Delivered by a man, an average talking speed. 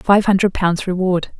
No: female; average, 170 wpm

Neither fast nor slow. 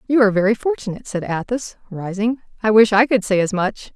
No: fast, 215 wpm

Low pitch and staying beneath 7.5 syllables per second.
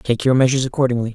No: low, 125 Hz; 8.1 syllables/s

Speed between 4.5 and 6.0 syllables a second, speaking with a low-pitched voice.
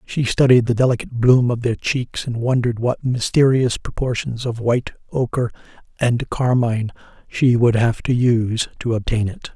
Yes: 5.1 syllables/s; low, 120 Hz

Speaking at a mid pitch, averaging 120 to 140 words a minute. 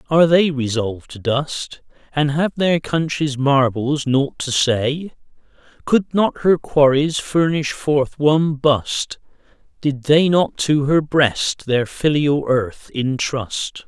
Yes: medium, 145 Hz; slow, 135 wpm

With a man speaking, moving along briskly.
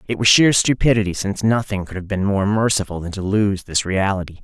Yes: male; fast, 215 wpm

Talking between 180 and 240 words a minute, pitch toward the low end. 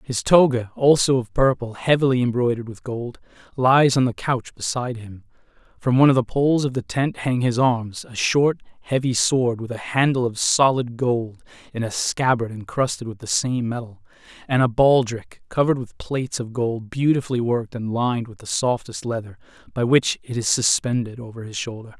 Yes: average, 185 wpm; low, 120 Hz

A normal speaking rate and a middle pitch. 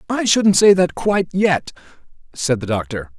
No: slow, 130 wpm; medium, 165 Hz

